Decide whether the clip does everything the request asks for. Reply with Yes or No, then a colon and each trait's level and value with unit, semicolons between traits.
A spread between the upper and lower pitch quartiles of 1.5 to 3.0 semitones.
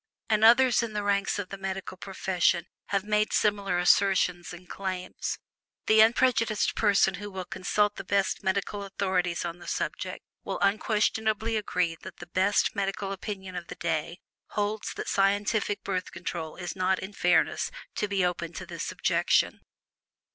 Yes: narrow, 2.4 semitones